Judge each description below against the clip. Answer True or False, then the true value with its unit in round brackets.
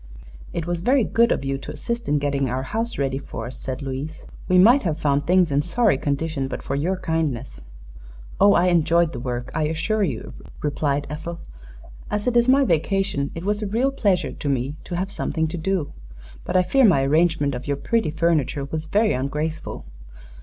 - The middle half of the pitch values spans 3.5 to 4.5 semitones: False (5.5 semitones)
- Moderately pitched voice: True (160 Hz)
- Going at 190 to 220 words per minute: True (200 wpm)